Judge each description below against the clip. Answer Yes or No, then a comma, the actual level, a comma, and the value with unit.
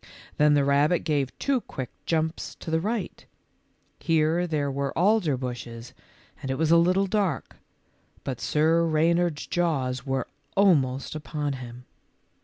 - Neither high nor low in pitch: Yes, medium, 155 Hz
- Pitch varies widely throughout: No, average, 4.0 semitones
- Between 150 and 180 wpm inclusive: No, average, 140 wpm